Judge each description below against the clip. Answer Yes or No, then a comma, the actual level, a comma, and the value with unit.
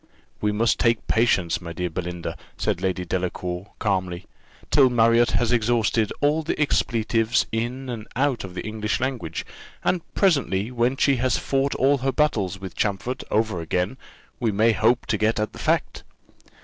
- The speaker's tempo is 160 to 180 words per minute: Yes, average, 165 wpm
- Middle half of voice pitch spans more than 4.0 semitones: Yes, average, 4.8 semitones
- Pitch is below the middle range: Yes, low, 110 Hz